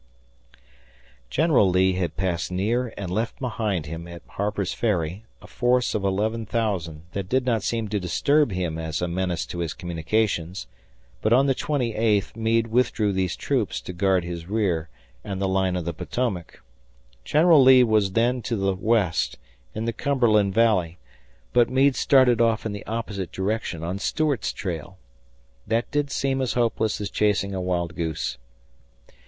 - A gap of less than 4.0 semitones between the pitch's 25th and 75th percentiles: No, average, 4.4 semitones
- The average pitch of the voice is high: No, low, 105 Hz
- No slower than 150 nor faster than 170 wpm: Yes, average, 165 wpm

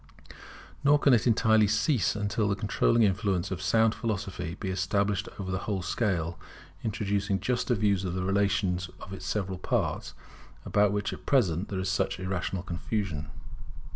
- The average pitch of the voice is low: Yes, low, 100 Hz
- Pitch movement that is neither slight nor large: No, narrow, 2.3 semitones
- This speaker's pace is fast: No, average, 160 wpm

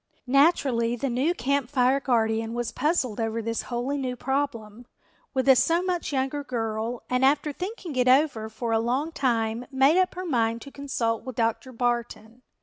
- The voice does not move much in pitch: No, average, 3.5 semitones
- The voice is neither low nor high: No, very high, 250 Hz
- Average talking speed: Yes, average, 175 wpm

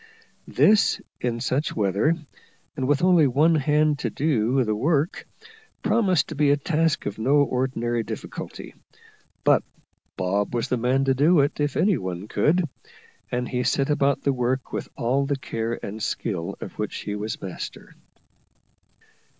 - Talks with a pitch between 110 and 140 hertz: Yes, low, 135 Hz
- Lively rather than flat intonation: No, average, 4.3 semitones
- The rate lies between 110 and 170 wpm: Yes, average, 160 wpm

